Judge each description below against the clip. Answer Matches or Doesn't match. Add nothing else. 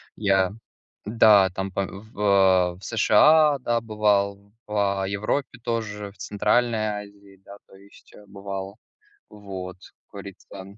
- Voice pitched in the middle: Doesn't match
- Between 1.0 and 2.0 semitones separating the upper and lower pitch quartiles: Matches